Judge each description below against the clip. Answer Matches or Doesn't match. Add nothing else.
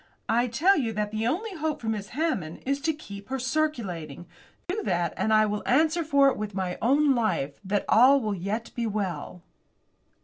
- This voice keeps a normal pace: Matches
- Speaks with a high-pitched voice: Matches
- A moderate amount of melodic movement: Doesn't match